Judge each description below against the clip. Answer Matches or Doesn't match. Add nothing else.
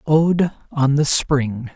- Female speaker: Doesn't match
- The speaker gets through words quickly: Doesn't match